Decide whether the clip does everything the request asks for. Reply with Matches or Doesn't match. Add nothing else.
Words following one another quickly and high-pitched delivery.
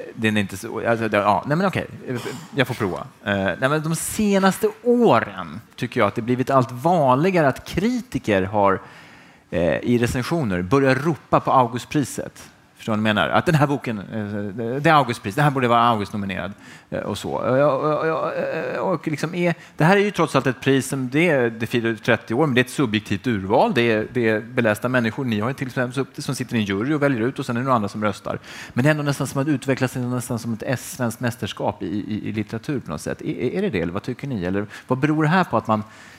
Doesn't match